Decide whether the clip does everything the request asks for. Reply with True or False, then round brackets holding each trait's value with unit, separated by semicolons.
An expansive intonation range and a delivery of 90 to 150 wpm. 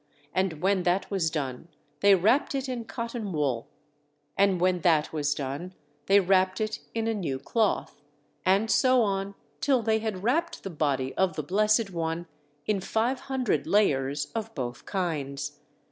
False (6.3 semitones; 160 wpm)